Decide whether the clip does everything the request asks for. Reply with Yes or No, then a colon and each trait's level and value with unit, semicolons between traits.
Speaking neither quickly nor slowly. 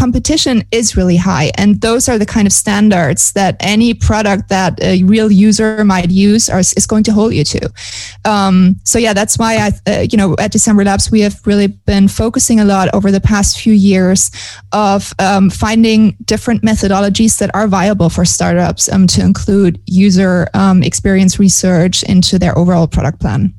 Yes: average, 185 wpm